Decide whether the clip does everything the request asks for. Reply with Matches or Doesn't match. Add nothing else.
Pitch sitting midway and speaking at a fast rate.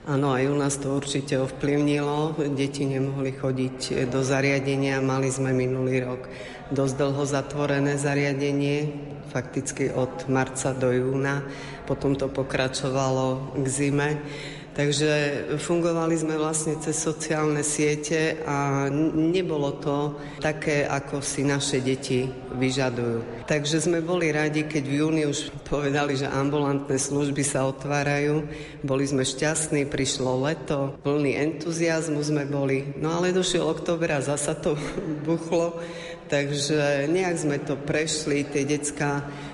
Doesn't match